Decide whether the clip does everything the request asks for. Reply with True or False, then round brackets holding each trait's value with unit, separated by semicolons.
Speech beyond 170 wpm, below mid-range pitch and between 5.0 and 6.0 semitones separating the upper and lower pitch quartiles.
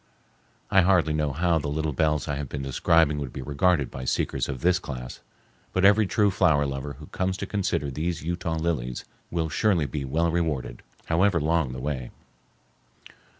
False (180 wpm; 80 Hz; 3.7 semitones)